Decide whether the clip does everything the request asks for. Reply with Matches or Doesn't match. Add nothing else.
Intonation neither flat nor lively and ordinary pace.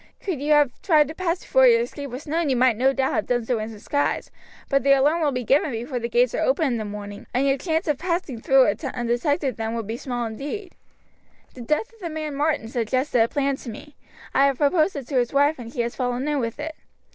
Doesn't match